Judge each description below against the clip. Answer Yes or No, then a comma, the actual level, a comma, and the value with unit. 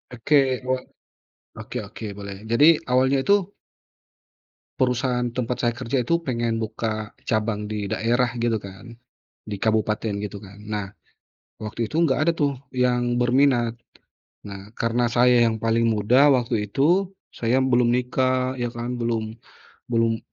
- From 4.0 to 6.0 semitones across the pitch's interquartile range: No, narrow, 2.4 semitones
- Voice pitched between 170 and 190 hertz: No, low, 120 Hz